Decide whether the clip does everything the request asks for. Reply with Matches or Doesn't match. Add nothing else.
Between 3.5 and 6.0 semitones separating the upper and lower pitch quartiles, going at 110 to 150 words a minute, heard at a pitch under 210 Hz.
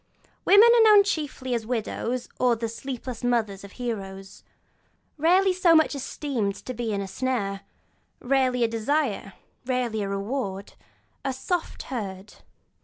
Doesn't match